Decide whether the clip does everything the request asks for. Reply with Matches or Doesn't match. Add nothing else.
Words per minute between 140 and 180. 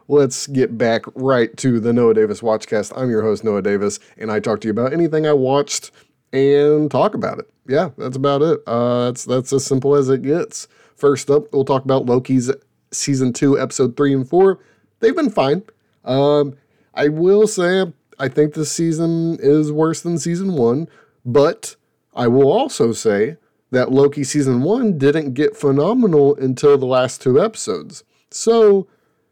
Matches